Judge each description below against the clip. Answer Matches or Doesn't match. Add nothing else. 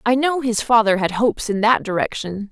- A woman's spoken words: Matches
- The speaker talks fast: Matches